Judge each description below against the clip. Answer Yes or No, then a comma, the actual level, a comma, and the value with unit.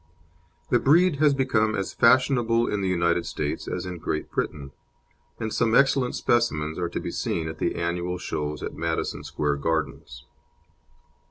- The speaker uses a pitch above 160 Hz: No, very low, 95 Hz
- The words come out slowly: No, average, 160 wpm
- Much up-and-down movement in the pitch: Yes, wide, 7.2 semitones